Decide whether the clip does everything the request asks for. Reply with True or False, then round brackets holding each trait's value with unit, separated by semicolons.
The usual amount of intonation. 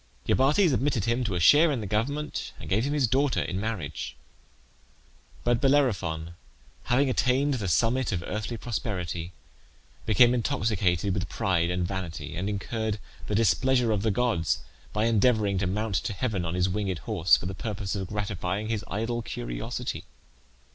True (4.7 semitones)